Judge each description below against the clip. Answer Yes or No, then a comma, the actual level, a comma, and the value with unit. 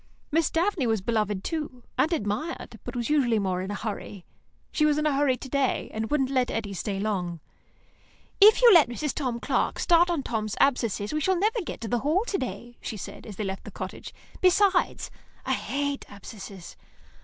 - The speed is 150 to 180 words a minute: No, average, 200 wpm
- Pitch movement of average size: No, wide, 6.4 semitones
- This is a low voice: No, very high, 255 Hz